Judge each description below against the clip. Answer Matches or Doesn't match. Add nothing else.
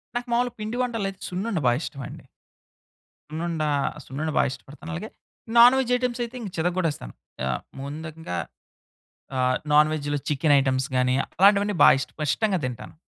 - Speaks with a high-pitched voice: Doesn't match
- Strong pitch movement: Matches